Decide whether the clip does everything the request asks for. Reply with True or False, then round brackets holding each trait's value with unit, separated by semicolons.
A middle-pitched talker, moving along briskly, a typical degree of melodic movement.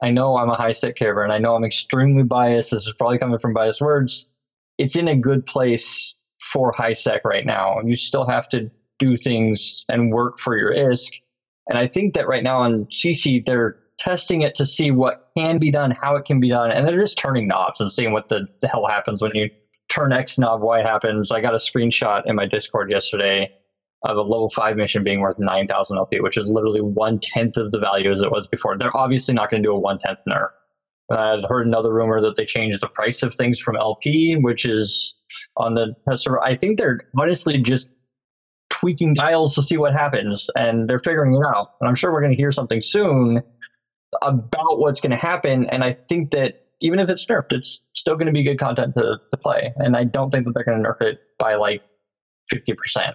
False (120 Hz; 230 wpm; 3.8 semitones)